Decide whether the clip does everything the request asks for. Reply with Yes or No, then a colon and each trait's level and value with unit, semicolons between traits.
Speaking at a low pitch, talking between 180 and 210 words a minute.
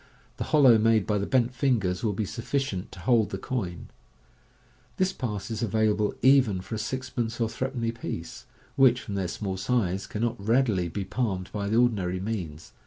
Yes: low, 110 Hz; average, 185 wpm